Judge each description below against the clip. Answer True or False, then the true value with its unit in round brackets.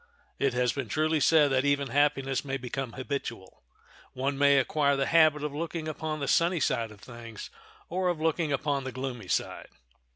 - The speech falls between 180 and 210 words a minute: True (185 wpm)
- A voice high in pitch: False (140 Hz)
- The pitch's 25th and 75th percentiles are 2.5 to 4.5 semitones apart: True (2.9 semitones)